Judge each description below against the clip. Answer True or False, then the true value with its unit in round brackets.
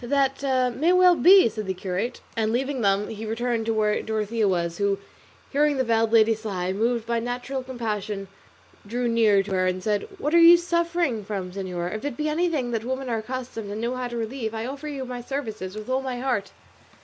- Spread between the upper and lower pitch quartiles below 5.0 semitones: True (4.0 semitones)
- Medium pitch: False (230 Hz)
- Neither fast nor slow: False (210 wpm)